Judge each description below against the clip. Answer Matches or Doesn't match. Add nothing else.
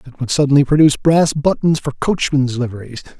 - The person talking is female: Doesn't match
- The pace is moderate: Matches